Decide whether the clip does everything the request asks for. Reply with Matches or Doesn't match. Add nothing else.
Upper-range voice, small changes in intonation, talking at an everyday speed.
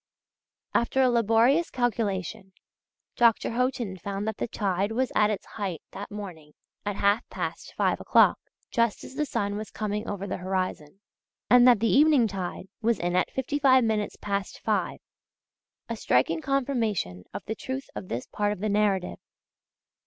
Doesn't match